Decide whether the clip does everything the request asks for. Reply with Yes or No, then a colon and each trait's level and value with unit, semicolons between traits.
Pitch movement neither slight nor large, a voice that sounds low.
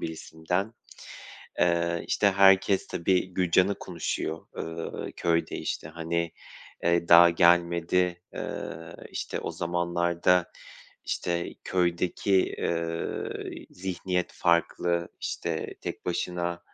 No: narrow, 1.1 semitones; very low, 85 Hz